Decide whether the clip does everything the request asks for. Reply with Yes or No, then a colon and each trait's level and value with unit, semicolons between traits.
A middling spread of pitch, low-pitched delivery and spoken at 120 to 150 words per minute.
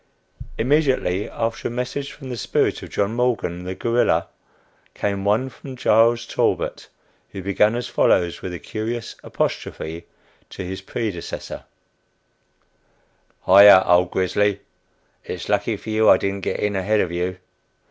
Yes: average, 4.1 semitones; low, 105 Hz; average, 145 wpm